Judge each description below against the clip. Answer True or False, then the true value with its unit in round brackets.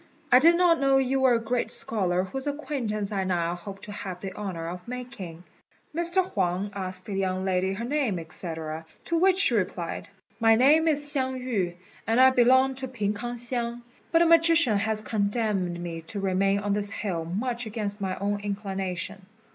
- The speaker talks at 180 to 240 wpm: True (185 wpm)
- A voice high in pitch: True (210 Hz)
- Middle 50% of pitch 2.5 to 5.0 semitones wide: False (5.5 semitones)